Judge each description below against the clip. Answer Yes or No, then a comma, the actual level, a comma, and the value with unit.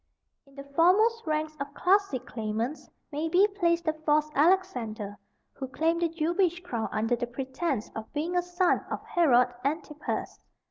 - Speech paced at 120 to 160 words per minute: Yes, average, 155 wpm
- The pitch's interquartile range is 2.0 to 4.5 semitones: No, average, 5.2 semitones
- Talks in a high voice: Yes, very high, 310 Hz